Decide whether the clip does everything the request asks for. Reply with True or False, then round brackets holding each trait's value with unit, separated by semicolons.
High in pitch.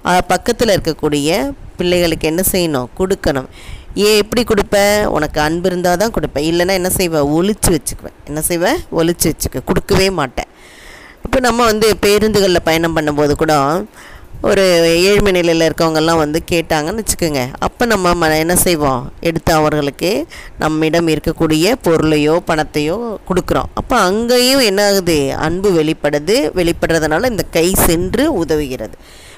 False (170 Hz)